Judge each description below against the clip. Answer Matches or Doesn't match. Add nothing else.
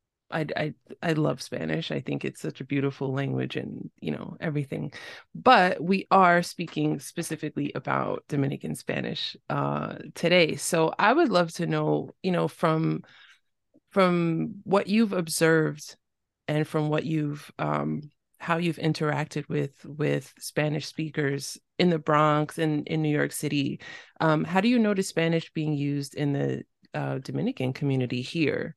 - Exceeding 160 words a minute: Doesn't match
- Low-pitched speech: Doesn't match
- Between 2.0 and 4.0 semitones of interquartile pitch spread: Matches